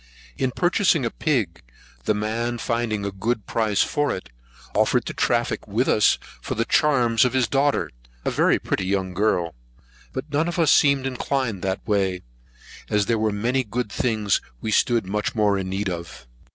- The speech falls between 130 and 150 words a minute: No, average, 180 wpm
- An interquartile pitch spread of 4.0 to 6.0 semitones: Yes, average, 4.6 semitones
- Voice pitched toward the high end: No, low, 110 Hz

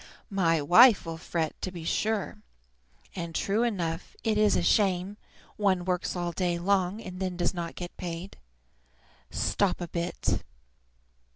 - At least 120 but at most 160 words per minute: Yes, average, 150 wpm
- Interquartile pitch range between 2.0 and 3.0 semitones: Yes, narrow, 2.6 semitones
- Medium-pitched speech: Yes, medium, 180 Hz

